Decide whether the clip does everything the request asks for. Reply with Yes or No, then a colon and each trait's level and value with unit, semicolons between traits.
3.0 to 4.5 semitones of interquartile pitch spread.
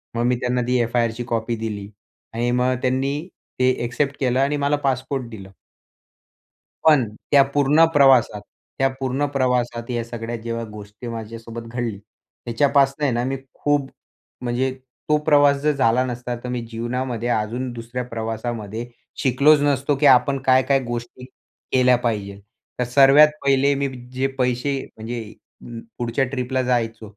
No: narrow, 2.6 semitones